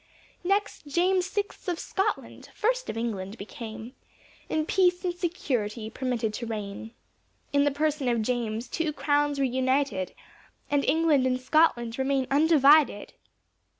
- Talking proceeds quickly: No, slow, 135 wpm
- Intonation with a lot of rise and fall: Yes, wide, 5.7 semitones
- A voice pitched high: Yes, very high, 275 Hz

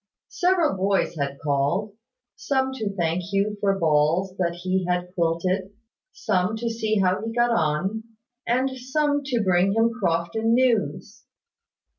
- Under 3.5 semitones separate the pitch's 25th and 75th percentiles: No, average, 4.6 semitones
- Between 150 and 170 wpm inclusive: No, average, 140 wpm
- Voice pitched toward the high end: Yes, high, 195 Hz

